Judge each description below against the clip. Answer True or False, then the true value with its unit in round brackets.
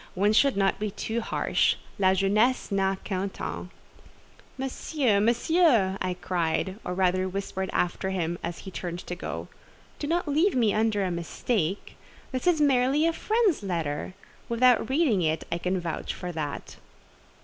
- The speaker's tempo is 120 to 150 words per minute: False (160 wpm)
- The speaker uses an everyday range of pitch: False (5.8 semitones)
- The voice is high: True (195 Hz)